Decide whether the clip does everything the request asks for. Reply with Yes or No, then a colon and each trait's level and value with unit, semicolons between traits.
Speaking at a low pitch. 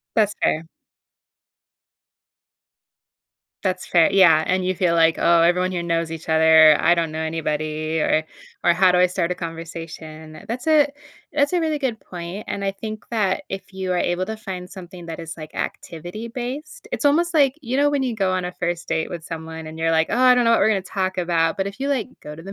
No: medium, 180 Hz